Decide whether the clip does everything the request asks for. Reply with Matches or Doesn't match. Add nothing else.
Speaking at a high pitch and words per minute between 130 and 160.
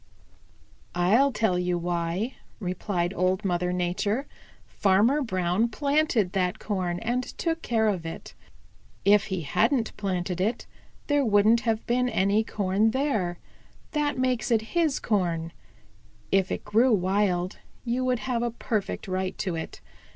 Matches